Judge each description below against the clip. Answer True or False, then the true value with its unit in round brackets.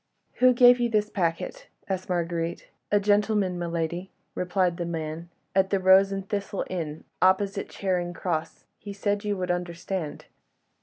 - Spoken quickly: False (155 wpm)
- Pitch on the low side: False (185 Hz)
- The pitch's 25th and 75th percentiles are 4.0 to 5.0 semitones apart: False (2.8 semitones)